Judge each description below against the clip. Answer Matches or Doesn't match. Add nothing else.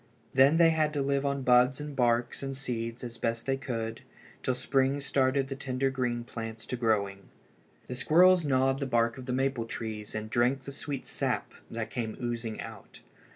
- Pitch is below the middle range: Matches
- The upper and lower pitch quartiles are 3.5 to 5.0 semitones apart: Doesn't match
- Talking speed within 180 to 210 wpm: Matches